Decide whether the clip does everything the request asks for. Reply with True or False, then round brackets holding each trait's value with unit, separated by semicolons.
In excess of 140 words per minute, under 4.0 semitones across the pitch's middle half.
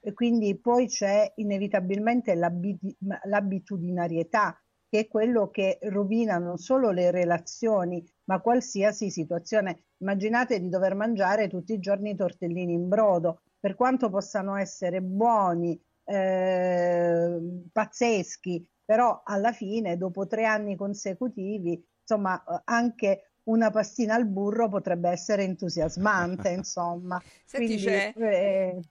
False (115 wpm; 3.4 semitones)